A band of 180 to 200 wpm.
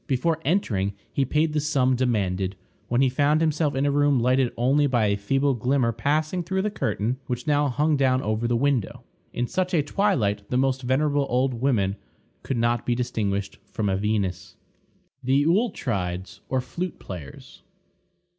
No: average, 170 wpm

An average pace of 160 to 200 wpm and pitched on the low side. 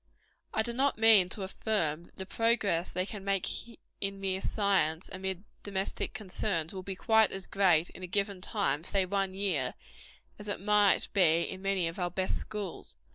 No: average, 185 wpm; high, 195 Hz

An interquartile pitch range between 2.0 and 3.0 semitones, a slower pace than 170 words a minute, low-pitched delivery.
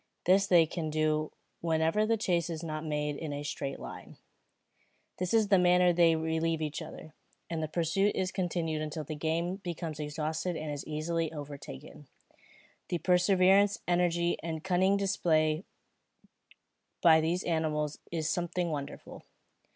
No: narrow, 2.5 semitones; average, 145 wpm; medium, 165 Hz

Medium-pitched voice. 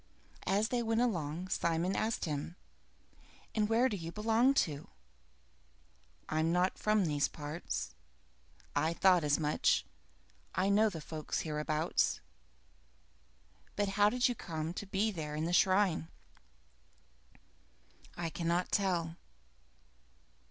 Yes: medium, 175 Hz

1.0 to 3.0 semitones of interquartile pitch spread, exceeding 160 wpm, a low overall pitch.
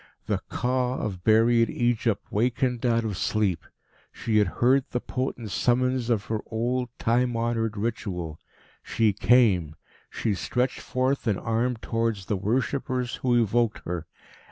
No: average, 2.7 semitones; average, 140 wpm; low, 115 Hz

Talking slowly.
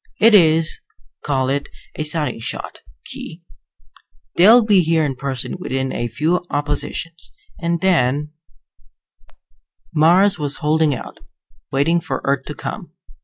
Yes: slow, 130 wpm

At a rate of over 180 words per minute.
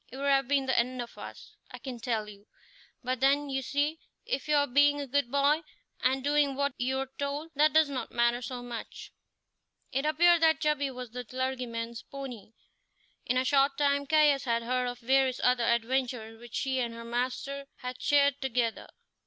Yes: average, 190 wpm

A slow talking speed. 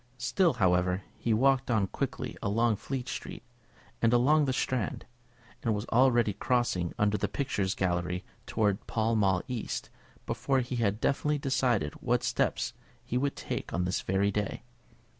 No: average, 155 wpm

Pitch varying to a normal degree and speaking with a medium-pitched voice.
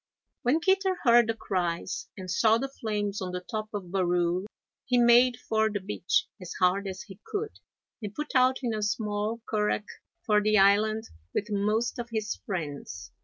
No: average, 3.5 semitones; high, 210 Hz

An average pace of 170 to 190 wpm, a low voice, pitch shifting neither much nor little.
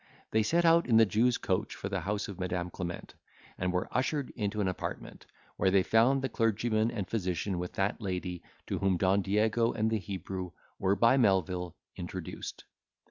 Yes: average, 185 wpm; low, 100 Hz; average, 3.6 semitones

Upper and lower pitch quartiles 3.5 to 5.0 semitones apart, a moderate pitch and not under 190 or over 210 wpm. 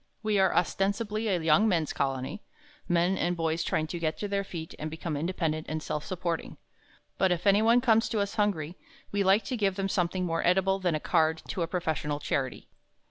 Yes: average, 3.8 semitones; medium, 180 Hz; average, 200 wpm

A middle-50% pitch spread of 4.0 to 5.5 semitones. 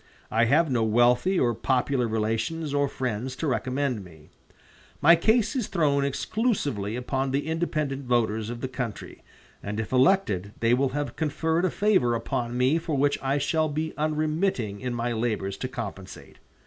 Yes: average, 4.8 semitones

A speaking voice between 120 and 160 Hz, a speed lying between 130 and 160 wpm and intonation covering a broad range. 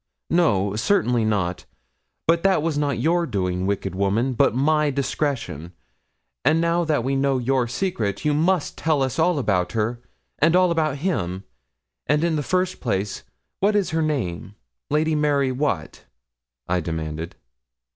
Yes: low, 135 Hz; average, 155 wpm; wide, 7.8 semitones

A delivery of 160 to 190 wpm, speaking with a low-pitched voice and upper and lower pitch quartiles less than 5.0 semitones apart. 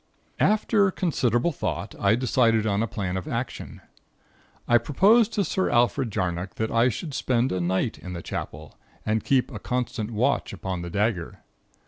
No: average, 165 wpm; low, 115 Hz; wide, 5.4 semitones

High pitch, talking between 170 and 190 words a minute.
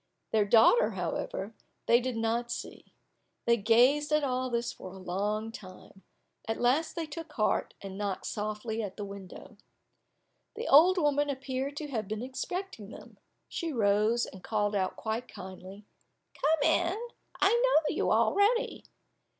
No: high, 235 Hz; average, 150 wpm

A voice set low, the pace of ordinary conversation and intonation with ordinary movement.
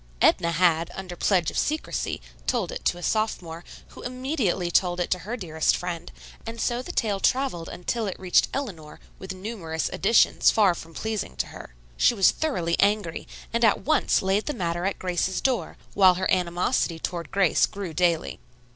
No: medium, 185 Hz; average, 180 wpm; average, 4.4 semitones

